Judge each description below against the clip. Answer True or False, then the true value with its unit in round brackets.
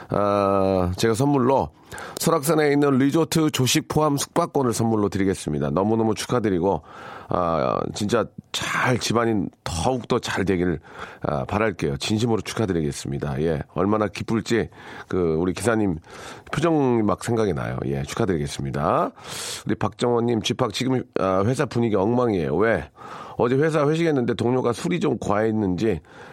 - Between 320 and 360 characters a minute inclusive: True (325 characters per minute)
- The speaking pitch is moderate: False (115 Hz)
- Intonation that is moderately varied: True (5.0 semitones)